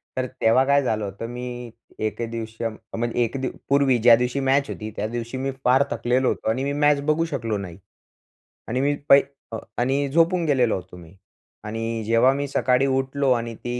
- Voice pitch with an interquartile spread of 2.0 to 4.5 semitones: Yes, average, 3.2 semitones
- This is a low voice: Yes, low, 125 Hz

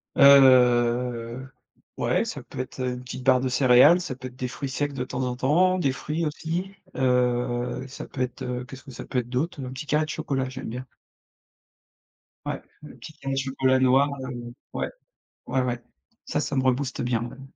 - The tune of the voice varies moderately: No, narrow, 1.8 semitones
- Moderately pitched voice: No, low, 130 Hz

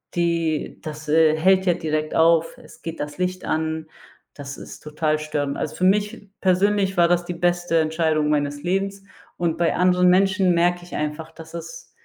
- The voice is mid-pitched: Yes, medium, 170 Hz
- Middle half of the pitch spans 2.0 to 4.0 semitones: Yes, average, 2.7 semitones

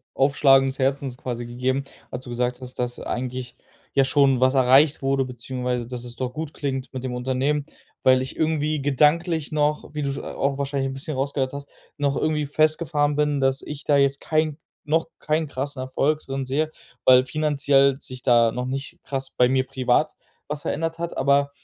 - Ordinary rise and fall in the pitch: No, narrow, 2.2 semitones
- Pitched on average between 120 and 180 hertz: Yes, low, 135 Hz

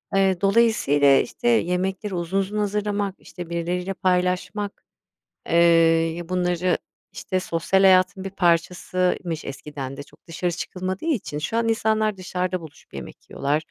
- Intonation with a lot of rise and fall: No, narrow, 2.5 semitones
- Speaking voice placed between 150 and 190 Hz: Yes, medium, 185 Hz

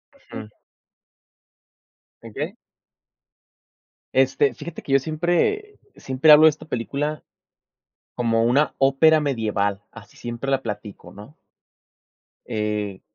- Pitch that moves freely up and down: Yes, wide, 5.8 semitones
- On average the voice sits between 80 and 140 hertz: Yes, low, 135 Hz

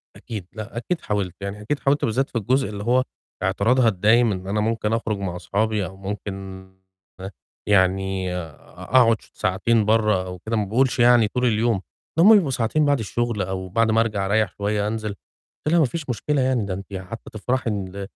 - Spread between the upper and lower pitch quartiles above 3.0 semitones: Yes, average, 3.5 semitones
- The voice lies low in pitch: Yes, low, 110 Hz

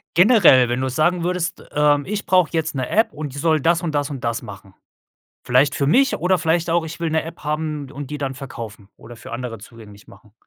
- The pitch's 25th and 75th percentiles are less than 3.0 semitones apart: No, average, 4.9 semitones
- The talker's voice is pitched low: No, medium, 150 Hz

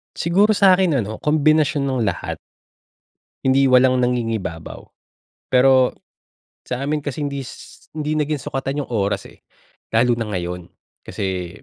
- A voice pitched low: Yes, low, 130 Hz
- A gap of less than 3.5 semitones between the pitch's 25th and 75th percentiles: No, average, 4.9 semitones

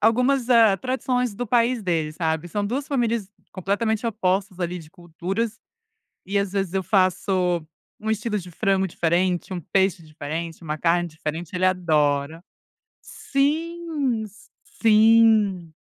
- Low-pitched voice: No, high, 195 Hz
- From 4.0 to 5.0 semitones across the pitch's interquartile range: Yes, average, 4.7 semitones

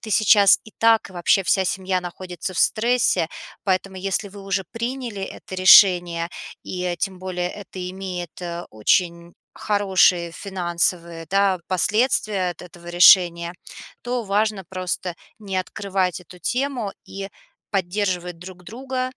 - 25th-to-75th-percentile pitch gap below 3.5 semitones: Yes, narrow, 2.4 semitones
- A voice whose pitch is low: No, medium, 185 Hz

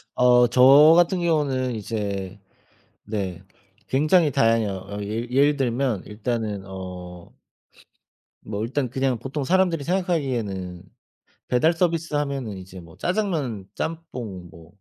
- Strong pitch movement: Yes, wide, 6.6 semitones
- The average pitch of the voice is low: Yes, low, 125 Hz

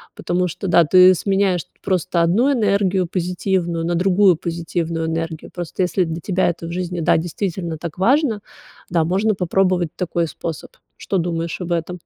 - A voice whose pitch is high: No, medium, 175 Hz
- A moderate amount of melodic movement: No, narrow, 2.1 semitones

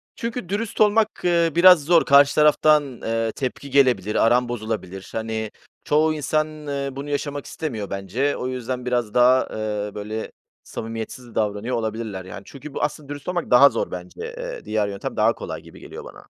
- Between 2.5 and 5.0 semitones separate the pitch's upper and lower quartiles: No, wide, 5.4 semitones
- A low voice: Yes, low, 130 Hz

